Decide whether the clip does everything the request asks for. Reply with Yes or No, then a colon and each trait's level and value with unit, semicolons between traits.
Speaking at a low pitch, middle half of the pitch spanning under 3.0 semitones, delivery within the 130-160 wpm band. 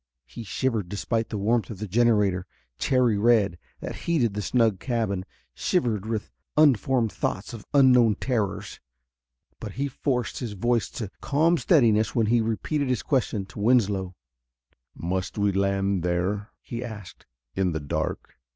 No: low, 110 Hz; average, 3.8 semitones; average, 150 wpm